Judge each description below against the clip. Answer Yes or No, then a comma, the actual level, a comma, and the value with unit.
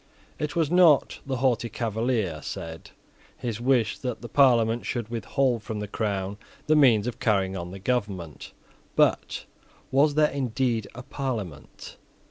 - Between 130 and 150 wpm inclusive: Yes, average, 145 wpm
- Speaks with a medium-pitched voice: No, low, 115 Hz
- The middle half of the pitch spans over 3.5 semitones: Yes, average, 4.3 semitones